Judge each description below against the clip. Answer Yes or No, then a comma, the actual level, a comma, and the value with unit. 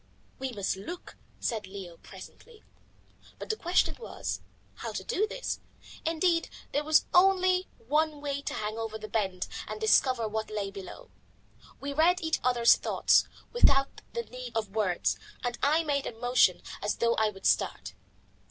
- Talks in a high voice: Yes, very high, 255 Hz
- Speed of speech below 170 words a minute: Yes, average, 160 wpm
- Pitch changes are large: Yes, wide, 7.6 semitones